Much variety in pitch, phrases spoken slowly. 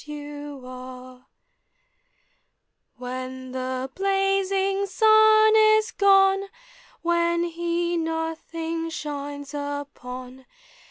Yes: wide, 6.7 semitones; slow, 65 wpm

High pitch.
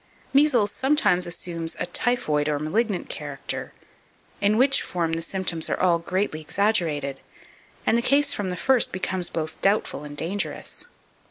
No: medium, 180 Hz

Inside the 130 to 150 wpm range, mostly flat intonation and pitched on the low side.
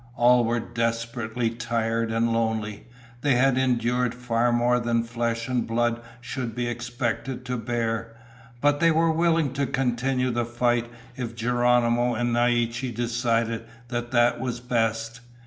Yes: average, 145 wpm; narrow, 1.2 semitones; low, 120 Hz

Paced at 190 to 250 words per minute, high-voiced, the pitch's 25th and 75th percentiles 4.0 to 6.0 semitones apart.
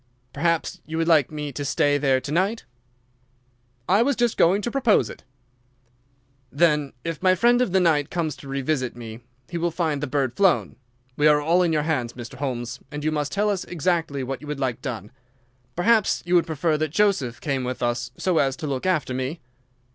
No: fast, 205 wpm; medium, 150 Hz; average, 4.5 semitones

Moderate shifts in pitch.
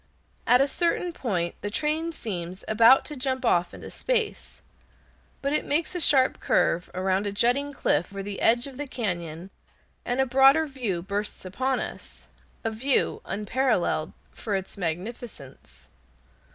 No: wide, 6.4 semitones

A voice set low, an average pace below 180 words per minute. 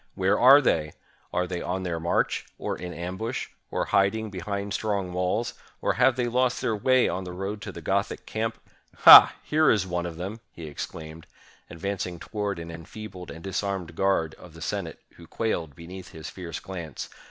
No: very low, 95 Hz; average, 185 wpm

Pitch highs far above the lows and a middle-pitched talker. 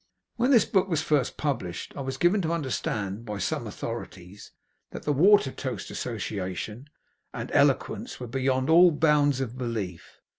No: wide, 6.3 semitones; low, 130 Hz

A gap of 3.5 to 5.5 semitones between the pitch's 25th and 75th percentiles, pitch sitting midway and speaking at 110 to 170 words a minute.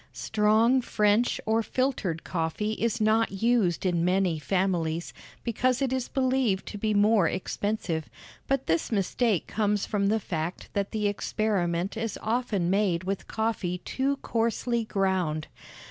No: average, 3.8 semitones; high, 210 Hz; average, 140 wpm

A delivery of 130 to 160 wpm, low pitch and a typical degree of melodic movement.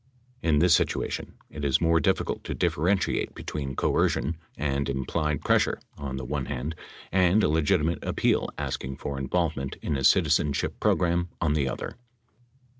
Yes: average, 150 wpm; very low, 75 Hz; average, 3.7 semitones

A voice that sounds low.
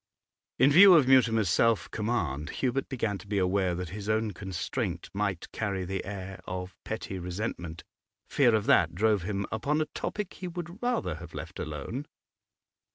Yes: low, 105 Hz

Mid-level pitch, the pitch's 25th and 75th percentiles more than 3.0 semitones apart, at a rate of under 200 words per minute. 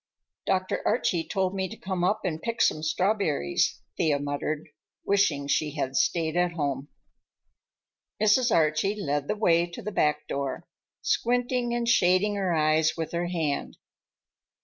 Yes: medium, 175 Hz; average, 4.6 semitones; average, 150 wpm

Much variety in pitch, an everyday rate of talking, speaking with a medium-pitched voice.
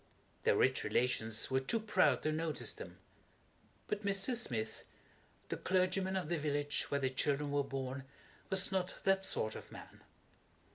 Yes: wide, 6.1 semitones; average, 160 wpm; medium, 150 Hz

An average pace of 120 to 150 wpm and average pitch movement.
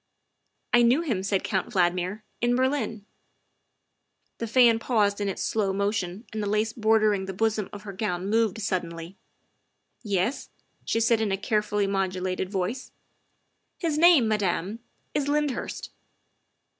No: average, 160 wpm; average, 3.1 semitones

